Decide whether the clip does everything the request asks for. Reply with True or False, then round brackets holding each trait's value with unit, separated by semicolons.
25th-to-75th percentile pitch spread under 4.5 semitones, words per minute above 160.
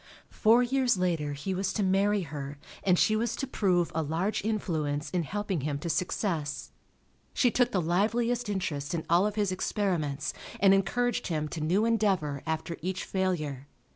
False (5.1 semitones; 170 wpm)